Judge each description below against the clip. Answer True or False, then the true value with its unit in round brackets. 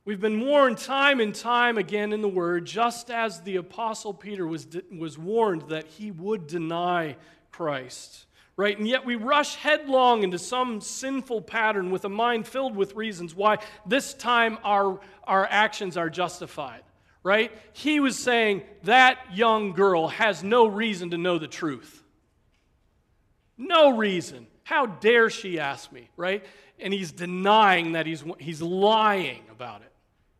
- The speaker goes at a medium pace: True (155 wpm)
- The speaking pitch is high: True (205 Hz)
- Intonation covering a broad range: False (4.9 semitones)